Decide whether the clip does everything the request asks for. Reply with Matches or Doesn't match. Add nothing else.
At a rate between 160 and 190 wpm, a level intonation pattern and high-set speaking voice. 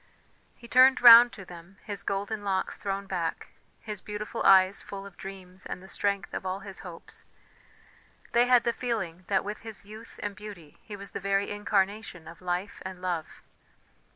Matches